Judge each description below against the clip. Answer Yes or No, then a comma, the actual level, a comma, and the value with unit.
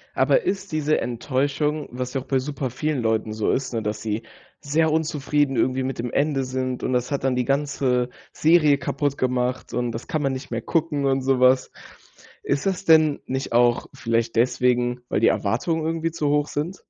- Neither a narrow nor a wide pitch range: Yes, average, 3.2 semitones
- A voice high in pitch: No, low, 135 Hz